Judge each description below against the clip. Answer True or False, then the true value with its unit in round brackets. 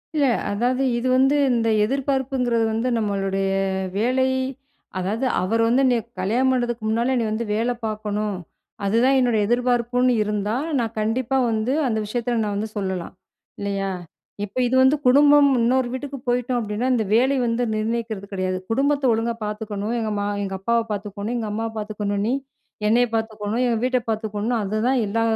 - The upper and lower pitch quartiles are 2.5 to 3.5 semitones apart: True (3.0 semitones)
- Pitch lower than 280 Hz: True (230 Hz)